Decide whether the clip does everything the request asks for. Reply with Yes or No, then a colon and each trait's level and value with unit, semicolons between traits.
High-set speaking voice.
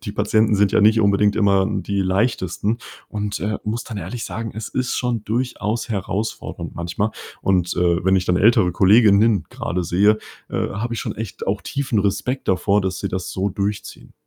No: low, 105 Hz